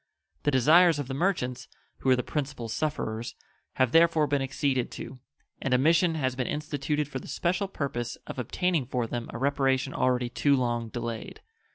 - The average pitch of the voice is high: No, low, 135 Hz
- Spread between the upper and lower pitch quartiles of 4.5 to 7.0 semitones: No, average, 3.3 semitones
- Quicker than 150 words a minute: Yes, average, 180 wpm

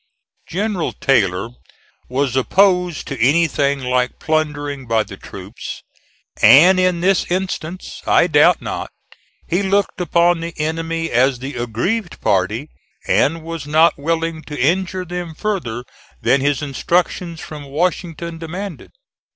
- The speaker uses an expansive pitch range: No, average, 4.3 semitones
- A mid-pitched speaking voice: Yes, medium, 160 Hz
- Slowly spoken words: Yes, slow, 125 wpm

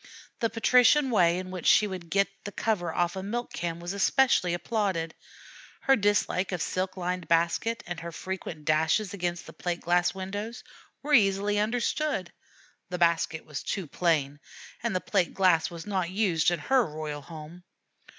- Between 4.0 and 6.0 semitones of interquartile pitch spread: No, average, 3.5 semitones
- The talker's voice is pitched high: No, medium, 180 Hz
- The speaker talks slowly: No, average, 170 wpm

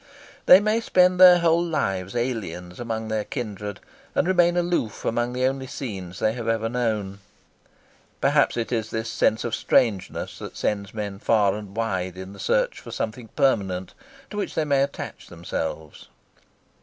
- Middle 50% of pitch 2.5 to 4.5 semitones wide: No, wide, 5.6 semitones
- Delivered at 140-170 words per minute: Yes, average, 165 wpm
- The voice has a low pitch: Yes, low, 115 Hz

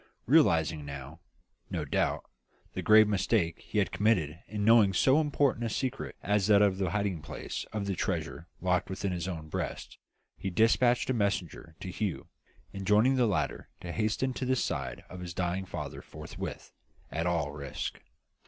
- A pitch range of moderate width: Yes, average, 4.4 semitones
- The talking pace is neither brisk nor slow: Yes, average, 170 wpm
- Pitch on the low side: Yes, low, 100 Hz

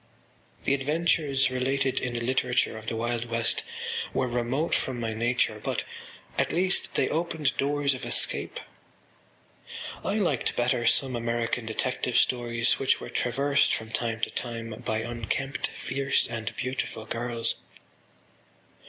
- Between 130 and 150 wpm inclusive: Yes, slow, 135 wpm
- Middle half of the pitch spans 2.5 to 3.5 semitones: Yes, average, 2.8 semitones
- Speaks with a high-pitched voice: No, low, 125 Hz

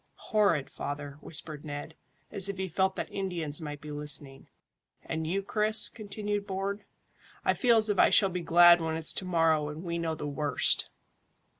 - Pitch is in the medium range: Yes, medium, 170 Hz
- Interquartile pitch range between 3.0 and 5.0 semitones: Yes, average, 4.7 semitones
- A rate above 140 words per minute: Yes, average, 180 wpm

